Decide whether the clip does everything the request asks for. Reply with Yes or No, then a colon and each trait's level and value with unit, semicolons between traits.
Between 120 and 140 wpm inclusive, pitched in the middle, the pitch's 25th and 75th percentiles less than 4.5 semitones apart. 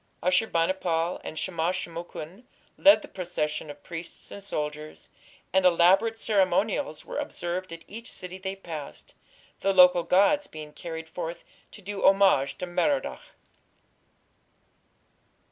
Yes: slow, 135 wpm; medium, 180 Hz; average, 3.0 semitones